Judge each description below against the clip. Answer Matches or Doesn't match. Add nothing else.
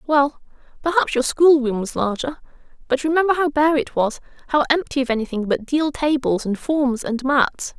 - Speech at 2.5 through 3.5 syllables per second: Doesn't match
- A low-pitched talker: Doesn't match